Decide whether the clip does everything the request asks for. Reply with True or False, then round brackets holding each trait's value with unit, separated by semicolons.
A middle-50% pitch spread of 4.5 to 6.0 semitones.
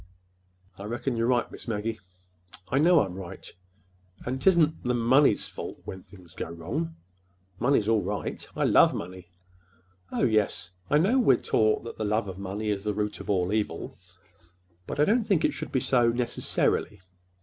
True (4.9 semitones)